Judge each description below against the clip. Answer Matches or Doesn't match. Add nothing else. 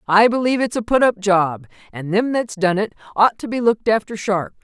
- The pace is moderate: Doesn't match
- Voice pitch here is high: Matches